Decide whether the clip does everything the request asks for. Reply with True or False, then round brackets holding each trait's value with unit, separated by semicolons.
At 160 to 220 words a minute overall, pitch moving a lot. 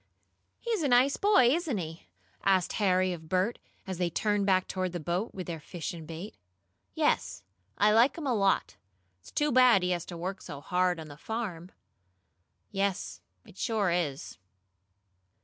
False (170 wpm; 4.5 semitones)